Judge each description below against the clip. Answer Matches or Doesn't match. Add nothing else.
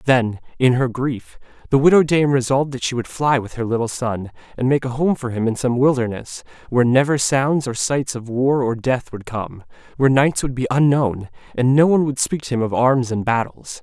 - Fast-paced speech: Matches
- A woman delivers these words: Doesn't match